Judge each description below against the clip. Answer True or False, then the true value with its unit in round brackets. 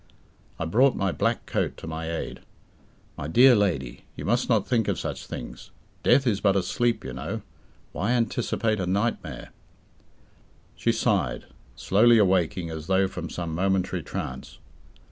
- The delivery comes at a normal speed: True (155 wpm)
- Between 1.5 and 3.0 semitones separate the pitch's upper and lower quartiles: False (5.4 semitones)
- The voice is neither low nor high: False (95 Hz)